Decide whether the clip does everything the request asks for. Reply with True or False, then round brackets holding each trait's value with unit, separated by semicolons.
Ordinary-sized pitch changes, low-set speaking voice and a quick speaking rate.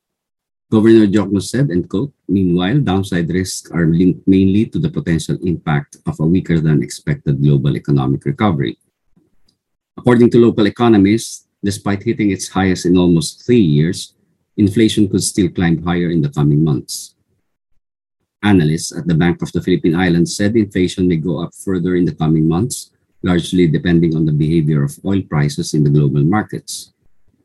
False (3.9 semitones; 90 Hz; 160 wpm)